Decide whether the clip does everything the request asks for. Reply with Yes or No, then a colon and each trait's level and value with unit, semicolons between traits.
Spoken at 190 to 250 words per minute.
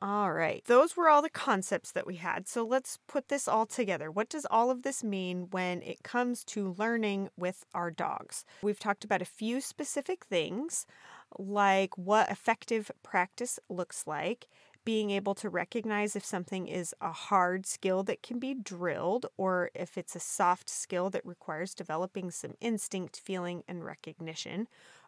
No: average, 170 wpm